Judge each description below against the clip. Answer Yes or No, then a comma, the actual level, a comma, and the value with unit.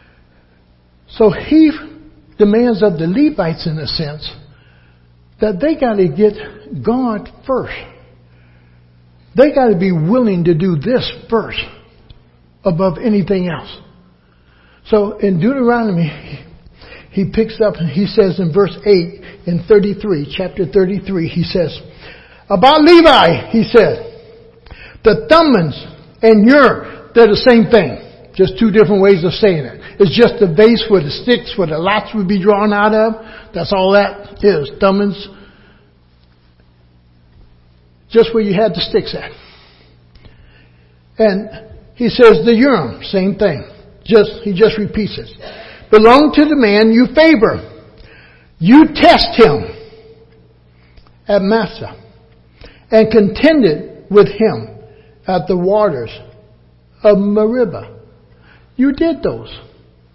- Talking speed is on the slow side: Yes, slow, 125 wpm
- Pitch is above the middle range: Yes, high, 195 Hz